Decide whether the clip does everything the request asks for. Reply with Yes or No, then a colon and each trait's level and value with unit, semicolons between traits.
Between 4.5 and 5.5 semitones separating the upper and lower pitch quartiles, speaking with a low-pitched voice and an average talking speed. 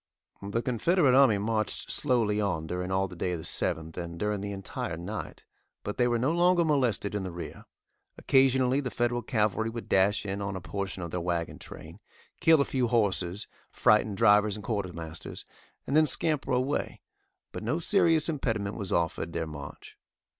Yes: average, 5.2 semitones; low, 105 Hz; average, 175 wpm